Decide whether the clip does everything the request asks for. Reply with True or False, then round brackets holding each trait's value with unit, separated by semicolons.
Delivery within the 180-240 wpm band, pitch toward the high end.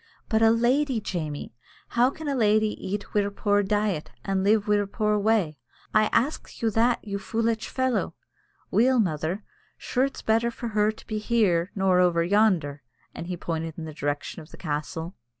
True (185 wpm; 210 Hz)